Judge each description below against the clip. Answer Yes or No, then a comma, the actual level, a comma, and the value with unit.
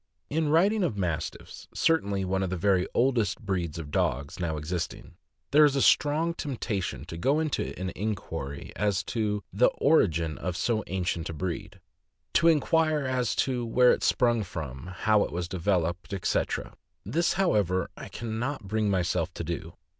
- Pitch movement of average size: No, wide, 6.9 semitones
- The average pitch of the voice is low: Yes, low, 100 Hz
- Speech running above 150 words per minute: Yes, average, 170 wpm